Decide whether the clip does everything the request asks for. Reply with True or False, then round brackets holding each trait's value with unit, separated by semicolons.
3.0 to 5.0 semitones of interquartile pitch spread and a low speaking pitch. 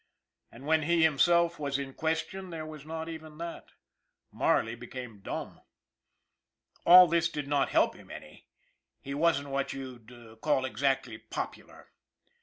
False (3.6 semitones; 145 Hz)